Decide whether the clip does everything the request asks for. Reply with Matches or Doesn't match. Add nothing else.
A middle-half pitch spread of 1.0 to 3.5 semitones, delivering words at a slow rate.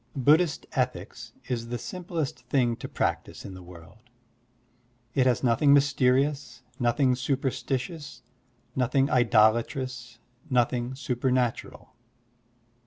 Matches